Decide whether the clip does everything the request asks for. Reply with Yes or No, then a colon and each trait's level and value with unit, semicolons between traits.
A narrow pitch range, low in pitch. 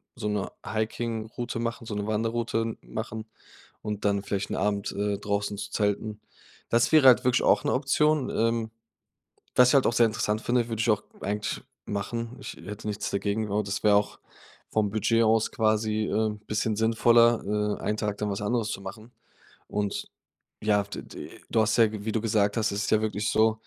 Yes: narrow, 1.8 semitones; low, 110 Hz